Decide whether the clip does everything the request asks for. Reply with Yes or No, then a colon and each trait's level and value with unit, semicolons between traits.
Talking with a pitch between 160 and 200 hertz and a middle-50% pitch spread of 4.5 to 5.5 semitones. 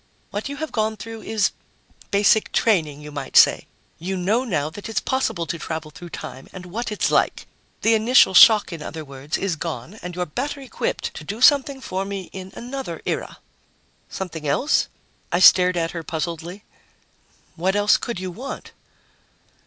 Yes: high, 190 Hz; average, 5.1 semitones